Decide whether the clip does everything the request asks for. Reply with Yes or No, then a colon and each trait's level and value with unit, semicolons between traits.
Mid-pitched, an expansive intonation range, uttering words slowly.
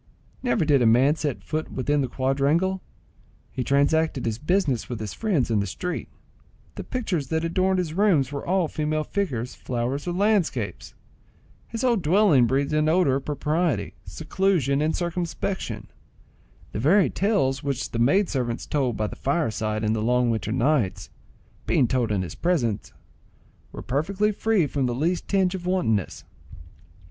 No: medium, 150 Hz; wide, 6.4 semitones; average, 160 wpm